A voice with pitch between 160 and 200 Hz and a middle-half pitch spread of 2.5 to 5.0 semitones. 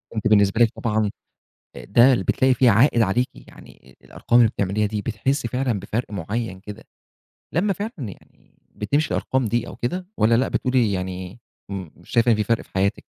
No: low, 115 Hz; average, 3.7 semitones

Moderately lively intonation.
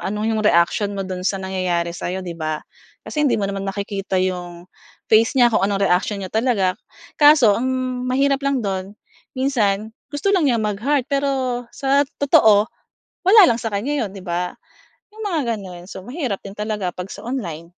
No: wide, 5.7 semitones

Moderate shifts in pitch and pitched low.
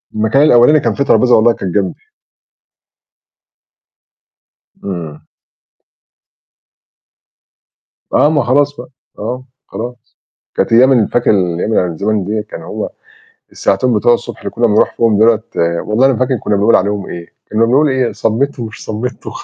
Yes: average, 3.5 semitones; low, 115 Hz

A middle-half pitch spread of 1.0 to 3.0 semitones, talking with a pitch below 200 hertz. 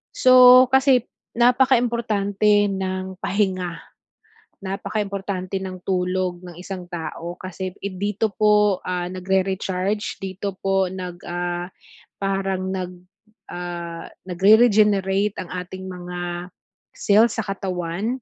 Yes: narrow, 2.4 semitones; high, 190 Hz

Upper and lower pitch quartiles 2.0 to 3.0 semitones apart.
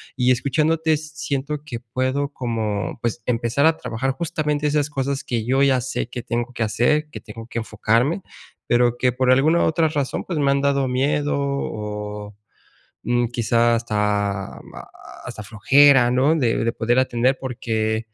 No: average, 3.5 semitones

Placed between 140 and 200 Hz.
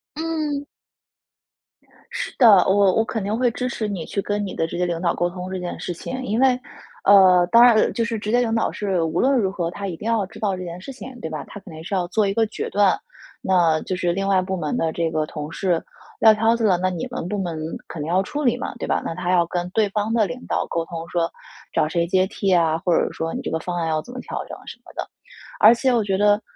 Yes: high, 190 Hz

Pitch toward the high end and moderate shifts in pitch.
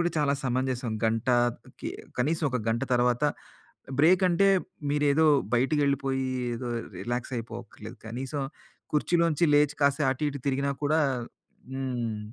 No: low, 135 Hz; average, 3.3 semitones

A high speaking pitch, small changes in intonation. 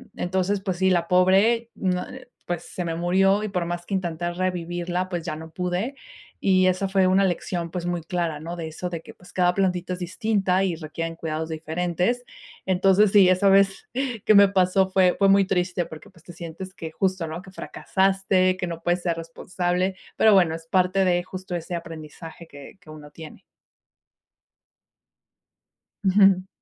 No: medium, 180 Hz; narrow, 2.1 semitones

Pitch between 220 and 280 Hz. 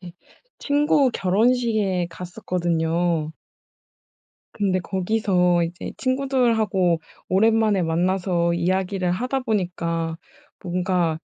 No: medium, 185 Hz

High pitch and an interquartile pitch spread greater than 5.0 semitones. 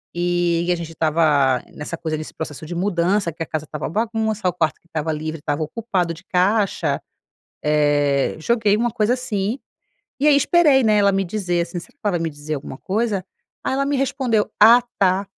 No: medium, 180 Hz; wide, 5.5 semitones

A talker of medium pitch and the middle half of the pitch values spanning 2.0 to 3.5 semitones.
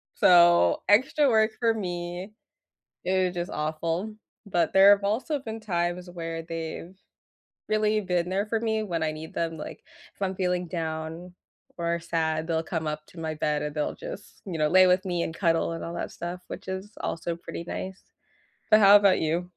Yes: medium, 175 Hz; average, 3.2 semitones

